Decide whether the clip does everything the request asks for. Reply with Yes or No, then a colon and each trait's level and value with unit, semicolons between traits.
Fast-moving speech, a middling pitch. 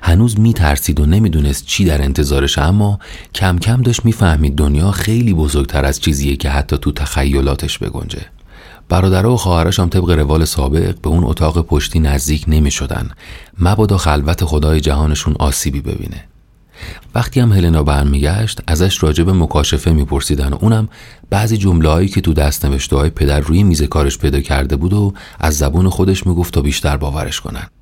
No: fast, 165 wpm; very low, 80 Hz